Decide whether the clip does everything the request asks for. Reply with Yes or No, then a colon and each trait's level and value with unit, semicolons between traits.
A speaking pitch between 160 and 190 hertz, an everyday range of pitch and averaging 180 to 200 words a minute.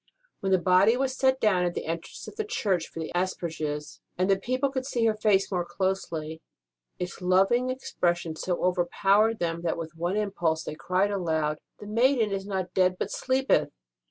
Yes: medium, 185 Hz; average, 4.0 semitones; average, 185 wpm